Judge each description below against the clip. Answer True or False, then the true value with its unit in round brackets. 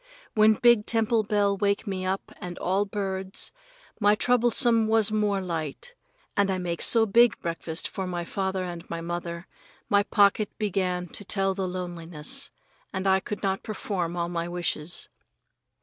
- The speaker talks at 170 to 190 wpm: False (160 wpm)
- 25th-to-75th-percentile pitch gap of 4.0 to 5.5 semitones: False (3.0 semitones)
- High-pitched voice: True (195 Hz)